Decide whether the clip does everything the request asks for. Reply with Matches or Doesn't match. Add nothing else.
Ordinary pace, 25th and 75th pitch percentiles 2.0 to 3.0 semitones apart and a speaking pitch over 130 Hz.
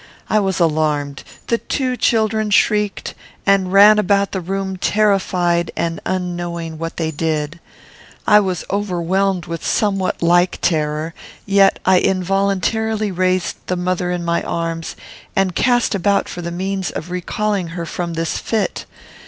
Matches